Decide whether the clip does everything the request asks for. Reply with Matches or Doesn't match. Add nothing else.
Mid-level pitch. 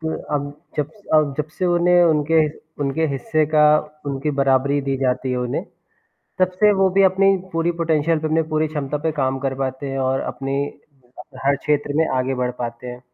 Matches